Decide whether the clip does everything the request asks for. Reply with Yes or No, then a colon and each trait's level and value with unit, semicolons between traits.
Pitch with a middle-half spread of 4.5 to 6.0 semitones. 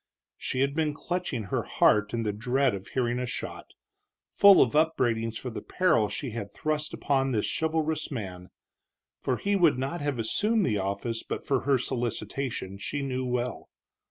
Yes: average, 5.0 semitones